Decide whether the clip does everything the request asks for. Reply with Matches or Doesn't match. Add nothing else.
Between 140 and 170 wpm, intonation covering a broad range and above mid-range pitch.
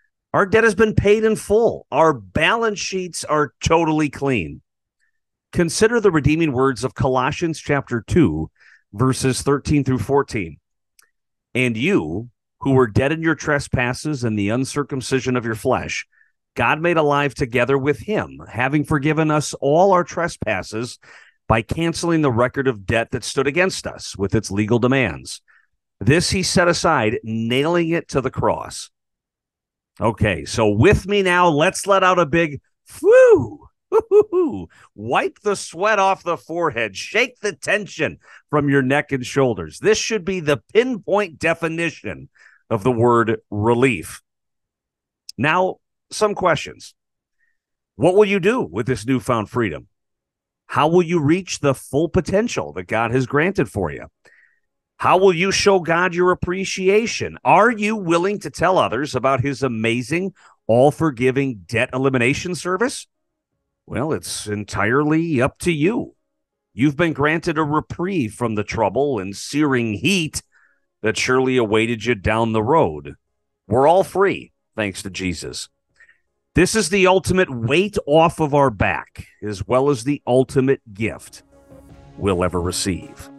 Doesn't match